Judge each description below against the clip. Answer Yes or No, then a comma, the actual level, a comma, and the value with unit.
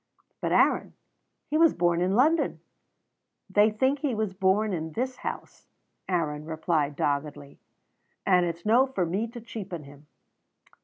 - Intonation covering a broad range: Yes, wide, 6.3 semitones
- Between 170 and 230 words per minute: No, average, 145 wpm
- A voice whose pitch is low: No, medium, 185 Hz